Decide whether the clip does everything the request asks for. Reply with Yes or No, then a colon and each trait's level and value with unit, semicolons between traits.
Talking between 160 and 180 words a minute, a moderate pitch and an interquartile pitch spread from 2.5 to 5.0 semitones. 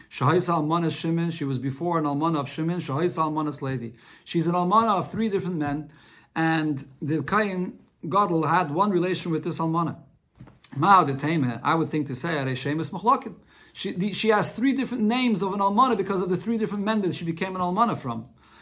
Yes: average, 175 wpm; medium, 170 Hz; average, 4.5 semitones